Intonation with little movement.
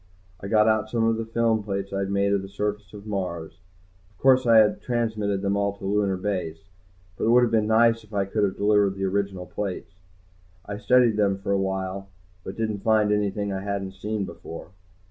Yes: narrow, 1.9 semitones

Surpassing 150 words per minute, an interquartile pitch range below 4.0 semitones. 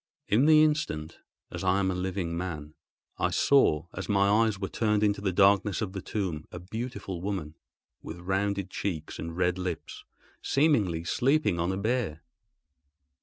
Yes: average, 165 wpm; average, 3.4 semitones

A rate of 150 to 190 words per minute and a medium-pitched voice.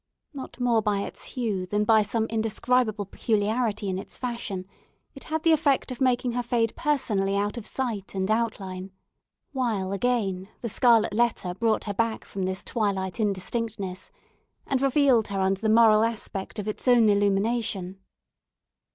No: average, 160 wpm; high, 220 Hz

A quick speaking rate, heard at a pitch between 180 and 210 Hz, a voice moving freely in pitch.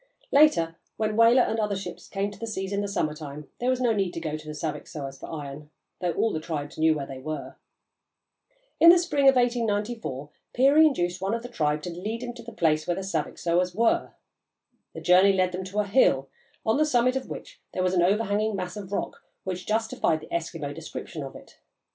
Yes: fast, 220 wpm; high, 190 Hz; wide, 6.3 semitones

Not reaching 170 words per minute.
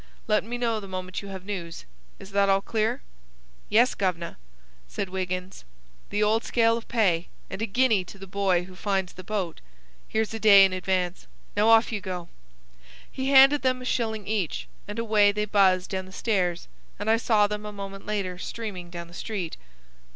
No: average, 190 wpm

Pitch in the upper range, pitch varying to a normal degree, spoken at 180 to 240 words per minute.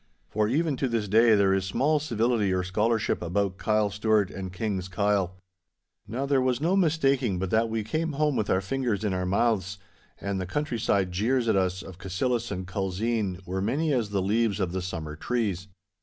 No: low, 105 Hz; average, 4.2 semitones; average, 195 wpm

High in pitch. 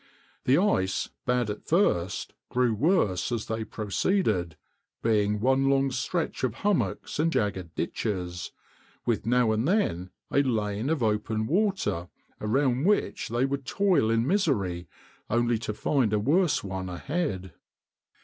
No: low, 115 Hz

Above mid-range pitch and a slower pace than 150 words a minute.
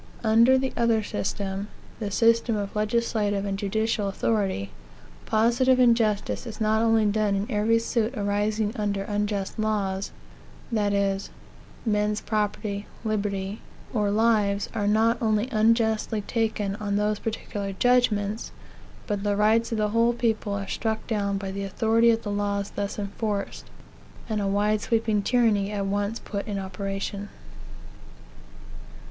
Yes: high, 210 Hz; average, 140 wpm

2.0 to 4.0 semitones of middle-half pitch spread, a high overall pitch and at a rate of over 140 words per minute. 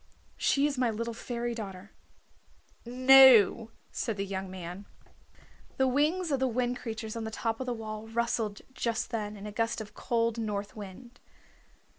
Yes: average, 2.8 semitones; high, 230 Hz; average, 165 wpm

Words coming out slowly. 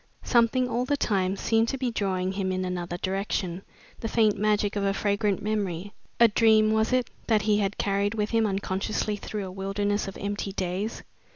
No: average, 190 wpm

